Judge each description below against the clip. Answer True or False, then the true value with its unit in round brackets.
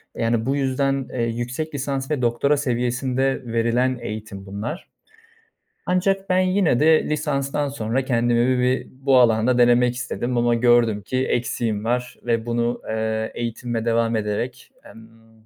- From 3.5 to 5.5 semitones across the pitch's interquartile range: False (2.7 semitones)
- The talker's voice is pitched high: False (120 Hz)